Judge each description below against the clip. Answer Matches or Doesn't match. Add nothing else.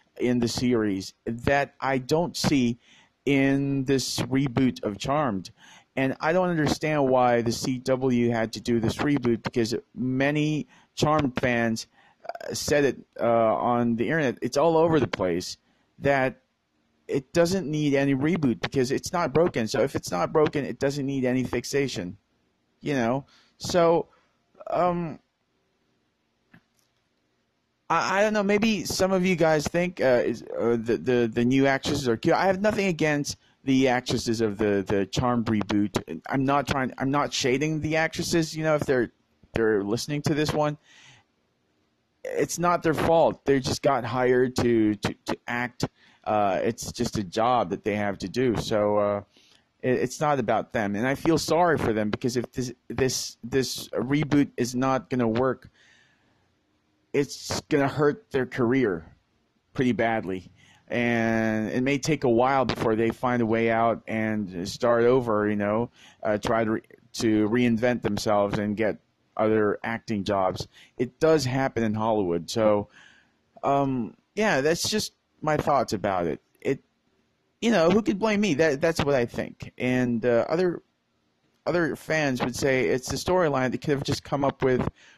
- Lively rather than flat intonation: Doesn't match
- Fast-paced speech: Doesn't match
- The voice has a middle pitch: Doesn't match